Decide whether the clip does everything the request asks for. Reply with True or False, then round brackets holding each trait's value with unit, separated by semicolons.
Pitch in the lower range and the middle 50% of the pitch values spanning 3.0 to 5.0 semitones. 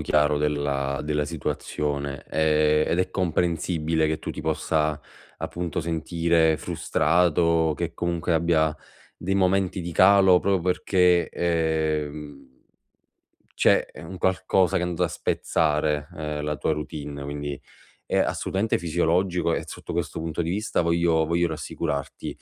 False (80 Hz; 2.5 semitones)